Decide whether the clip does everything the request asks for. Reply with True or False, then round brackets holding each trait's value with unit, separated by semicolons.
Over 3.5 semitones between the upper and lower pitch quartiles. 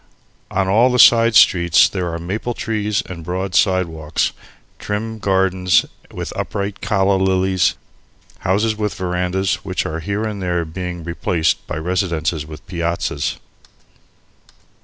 False (2.9 semitones)